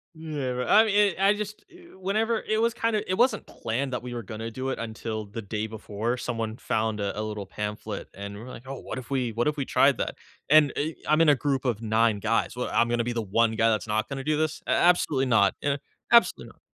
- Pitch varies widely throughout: Yes, wide, 5.7 semitones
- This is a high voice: No, low, 125 Hz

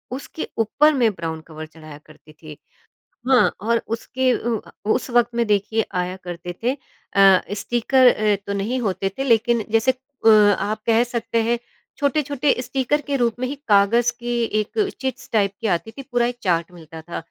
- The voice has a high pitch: Yes, high, 225 Hz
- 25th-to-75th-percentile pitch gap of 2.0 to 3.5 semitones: No, average, 4.0 semitones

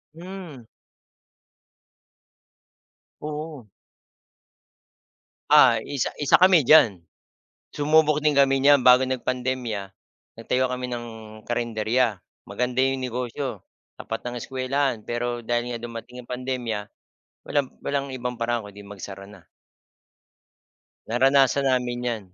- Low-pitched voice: Yes, low, 125 Hz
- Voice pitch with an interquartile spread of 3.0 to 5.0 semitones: No, narrow, 2.6 semitones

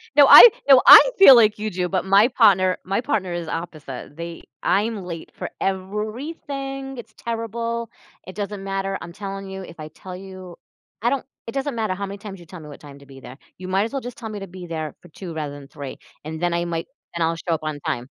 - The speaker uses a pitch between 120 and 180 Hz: No, high, 190 Hz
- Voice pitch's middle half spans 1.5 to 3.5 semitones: No, average, 4.8 semitones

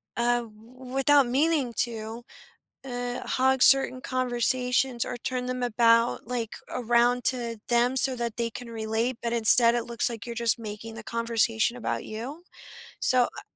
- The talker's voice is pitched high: Yes, high, 240 Hz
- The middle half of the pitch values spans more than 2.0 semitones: No, narrow, 1.6 semitones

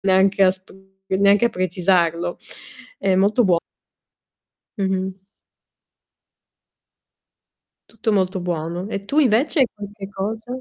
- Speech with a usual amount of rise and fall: No, narrow, 2.2 semitones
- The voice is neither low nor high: No, high, 195 Hz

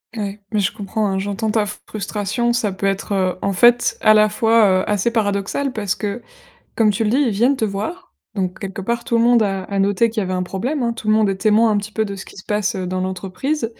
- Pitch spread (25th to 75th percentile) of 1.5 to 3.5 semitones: Yes, average, 2.8 semitones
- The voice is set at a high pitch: Yes, high, 210 Hz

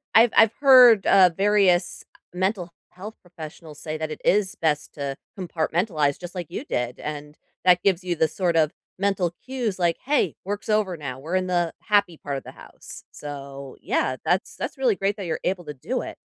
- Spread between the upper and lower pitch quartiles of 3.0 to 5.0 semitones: Yes, average, 4.6 semitones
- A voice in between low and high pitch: Yes, medium, 175 Hz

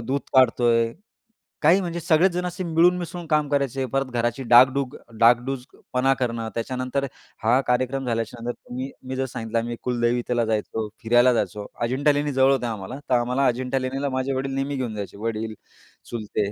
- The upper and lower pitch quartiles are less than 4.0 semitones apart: Yes, average, 2.7 semitones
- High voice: No, low, 130 Hz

